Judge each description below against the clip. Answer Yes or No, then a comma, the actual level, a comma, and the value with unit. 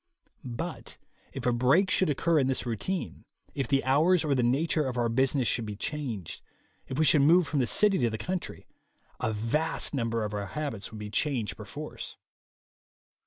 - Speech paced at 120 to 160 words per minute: No, average, 185 wpm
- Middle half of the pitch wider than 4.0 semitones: Yes, average, 5.2 semitones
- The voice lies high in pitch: No, low, 135 Hz